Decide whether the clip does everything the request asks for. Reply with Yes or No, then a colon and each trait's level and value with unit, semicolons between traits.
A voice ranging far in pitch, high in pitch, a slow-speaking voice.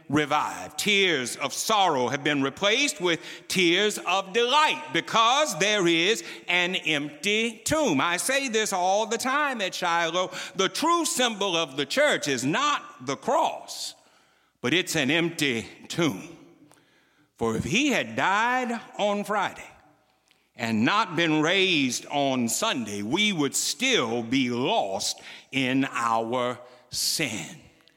No: wide, 7.8 semitones; medium, 180 Hz; slow, 130 wpm